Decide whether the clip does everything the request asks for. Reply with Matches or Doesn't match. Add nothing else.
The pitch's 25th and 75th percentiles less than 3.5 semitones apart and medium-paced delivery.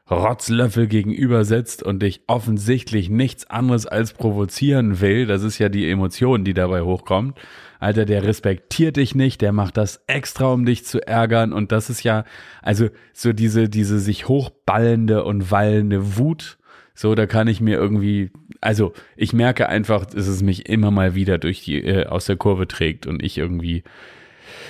Matches